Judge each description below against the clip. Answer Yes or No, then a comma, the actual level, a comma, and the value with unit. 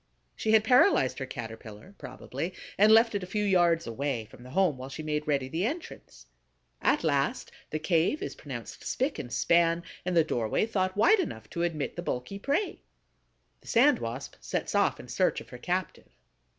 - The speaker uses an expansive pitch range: Yes, wide, 8.2 semitones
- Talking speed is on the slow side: No, average, 190 wpm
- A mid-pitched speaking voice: Yes, medium, 170 Hz